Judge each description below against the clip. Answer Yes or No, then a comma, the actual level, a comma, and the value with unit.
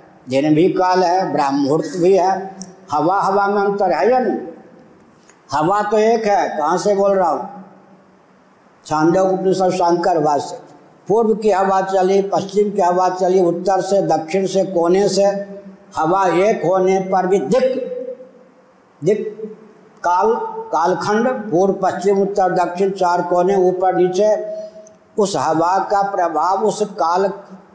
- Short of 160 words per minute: Yes, average, 140 wpm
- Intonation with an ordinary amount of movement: No, narrow, 2.2 semitones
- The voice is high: Yes, high, 195 Hz